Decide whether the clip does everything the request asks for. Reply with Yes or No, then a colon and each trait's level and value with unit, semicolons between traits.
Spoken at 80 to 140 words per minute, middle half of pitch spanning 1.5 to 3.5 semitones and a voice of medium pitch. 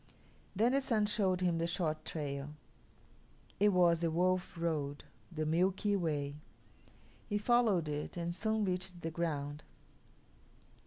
No: slow, 135 wpm; average, 3.9 semitones; medium, 170 Hz